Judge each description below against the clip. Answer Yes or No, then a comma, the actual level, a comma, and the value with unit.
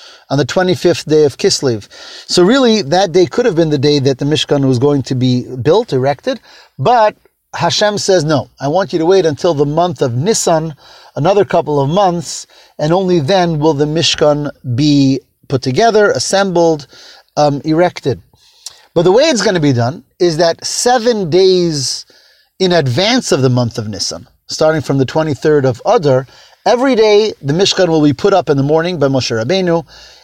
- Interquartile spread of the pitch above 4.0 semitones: Yes, average, 5.0 semitones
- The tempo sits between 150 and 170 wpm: No, average, 185 wpm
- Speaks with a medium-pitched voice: Yes, medium, 160 Hz